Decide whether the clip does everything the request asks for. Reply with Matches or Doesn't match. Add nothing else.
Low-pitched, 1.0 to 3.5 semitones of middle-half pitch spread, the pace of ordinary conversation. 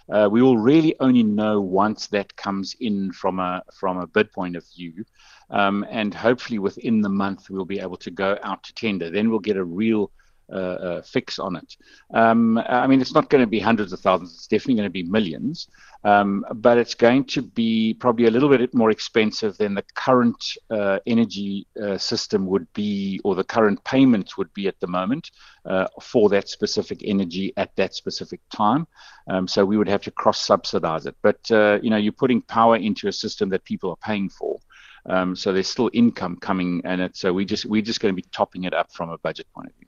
Doesn't match